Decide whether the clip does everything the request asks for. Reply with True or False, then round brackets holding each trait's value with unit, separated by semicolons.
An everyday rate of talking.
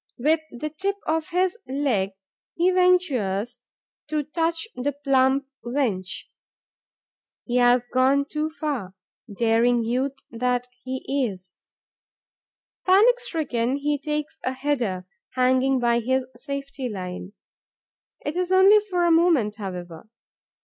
False (120 wpm)